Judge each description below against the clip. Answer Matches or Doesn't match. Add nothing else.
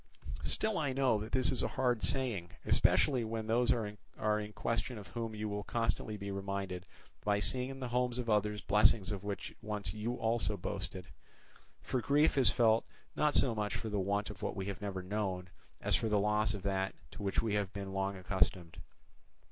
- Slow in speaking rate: Doesn't match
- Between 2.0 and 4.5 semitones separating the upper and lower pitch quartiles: Matches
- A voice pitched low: Matches